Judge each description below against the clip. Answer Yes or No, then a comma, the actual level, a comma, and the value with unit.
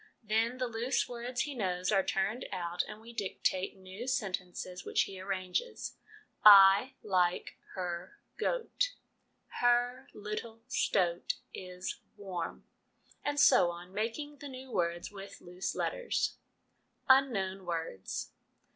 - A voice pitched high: Yes, high, 200 Hz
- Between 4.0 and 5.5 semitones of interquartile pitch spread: Yes, average, 5.1 semitones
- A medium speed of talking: No, slow, 130 wpm